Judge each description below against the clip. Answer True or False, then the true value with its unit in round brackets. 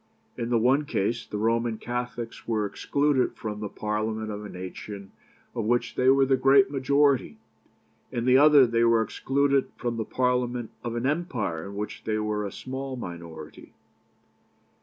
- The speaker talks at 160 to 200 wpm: True (165 wpm)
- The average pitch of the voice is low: True (120 Hz)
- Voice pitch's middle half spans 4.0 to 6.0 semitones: False (3.6 semitones)